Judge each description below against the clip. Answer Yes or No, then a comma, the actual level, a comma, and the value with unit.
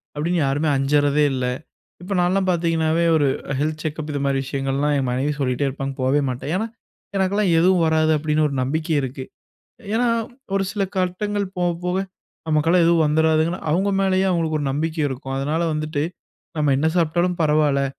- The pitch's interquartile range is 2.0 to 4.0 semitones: Yes, average, 3.5 semitones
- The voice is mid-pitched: Yes, medium, 155 Hz